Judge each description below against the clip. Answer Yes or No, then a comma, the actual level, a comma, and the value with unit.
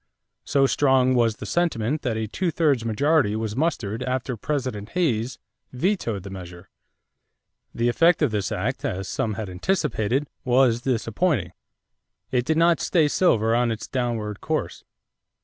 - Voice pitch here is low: Yes, low, 120 Hz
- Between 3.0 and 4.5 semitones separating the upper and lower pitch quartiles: No, average, 5.2 semitones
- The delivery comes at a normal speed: Yes, average, 150 wpm